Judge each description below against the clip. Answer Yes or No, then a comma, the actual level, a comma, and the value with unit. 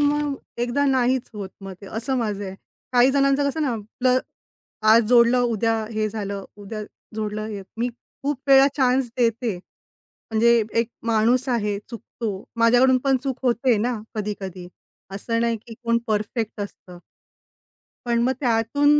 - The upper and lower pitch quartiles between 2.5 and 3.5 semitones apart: Yes, average, 3.2 semitones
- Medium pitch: No, high, 235 Hz